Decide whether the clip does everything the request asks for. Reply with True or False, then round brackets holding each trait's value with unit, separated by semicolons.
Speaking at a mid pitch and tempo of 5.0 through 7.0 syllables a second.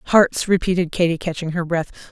True (175 Hz; 5.4 syllables/s)